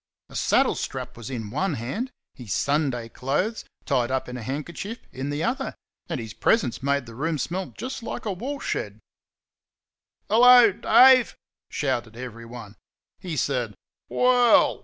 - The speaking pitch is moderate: Yes, medium, 145 Hz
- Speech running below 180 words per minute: Yes, average, 145 wpm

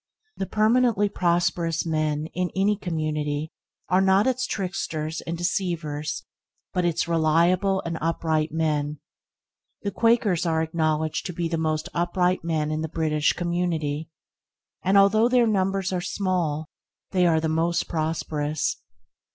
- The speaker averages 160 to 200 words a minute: No, slow, 135 wpm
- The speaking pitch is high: No, medium, 170 Hz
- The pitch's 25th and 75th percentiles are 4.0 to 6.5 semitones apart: No, average, 3.2 semitones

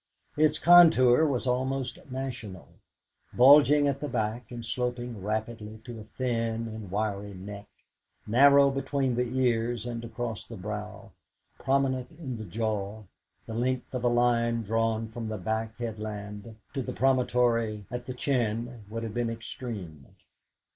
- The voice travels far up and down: No, average, 2.8 semitones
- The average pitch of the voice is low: Yes, low, 115 Hz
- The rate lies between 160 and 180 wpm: No, average, 145 wpm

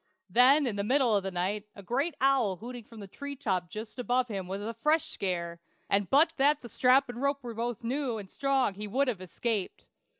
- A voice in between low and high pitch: No, high, 235 Hz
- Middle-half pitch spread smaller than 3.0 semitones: No, average, 5.1 semitones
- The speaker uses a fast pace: Yes, fast, 225 wpm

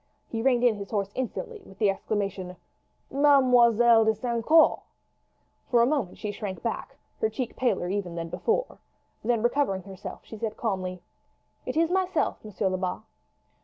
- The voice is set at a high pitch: Yes, high, 225 Hz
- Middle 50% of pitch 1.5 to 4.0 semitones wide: No, average, 4.6 semitones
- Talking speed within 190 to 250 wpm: No, average, 160 wpm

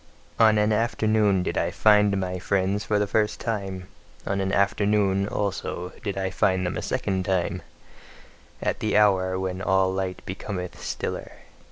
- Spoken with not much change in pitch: Yes, narrow, 1.9 semitones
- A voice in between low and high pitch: No, very low, 95 Hz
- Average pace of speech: Yes, average, 160 wpm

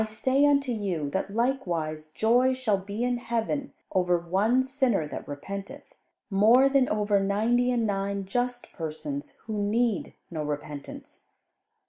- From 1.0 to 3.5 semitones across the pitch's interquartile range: No, average, 4.7 semitones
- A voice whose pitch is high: Yes, high, 215 Hz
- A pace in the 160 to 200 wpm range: No, average, 140 wpm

